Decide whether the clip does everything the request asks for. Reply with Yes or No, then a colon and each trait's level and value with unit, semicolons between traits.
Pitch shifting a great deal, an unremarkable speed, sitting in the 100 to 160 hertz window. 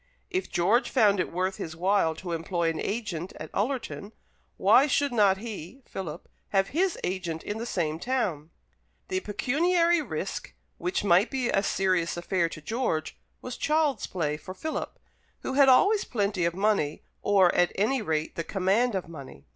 No: wide, 6.7 semitones; average, 170 wpm; high, 195 Hz